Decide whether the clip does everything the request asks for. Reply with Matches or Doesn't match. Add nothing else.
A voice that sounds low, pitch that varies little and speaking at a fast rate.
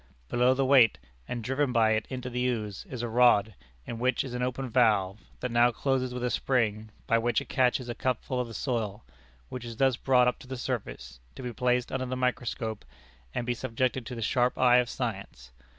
Matches